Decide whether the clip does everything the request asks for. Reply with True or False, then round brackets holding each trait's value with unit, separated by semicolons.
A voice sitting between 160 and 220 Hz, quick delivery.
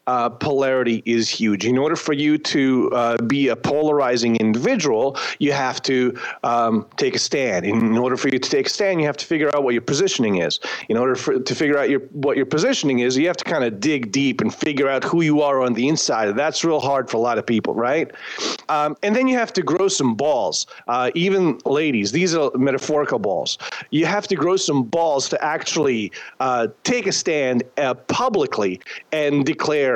False (140 Hz; 210 wpm)